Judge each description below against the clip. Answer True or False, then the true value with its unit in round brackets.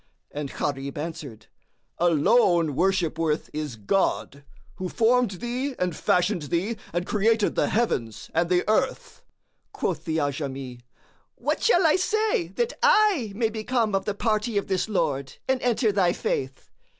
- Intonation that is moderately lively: False (7.5 semitones)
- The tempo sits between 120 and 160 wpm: True (150 wpm)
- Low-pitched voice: False (190 Hz)